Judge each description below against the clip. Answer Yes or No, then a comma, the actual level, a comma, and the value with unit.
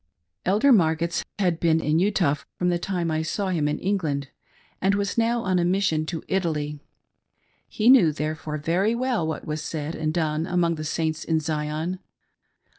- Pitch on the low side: No, medium, 165 Hz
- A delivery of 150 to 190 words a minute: Yes, average, 175 wpm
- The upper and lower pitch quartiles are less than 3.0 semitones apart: No, average, 3.5 semitones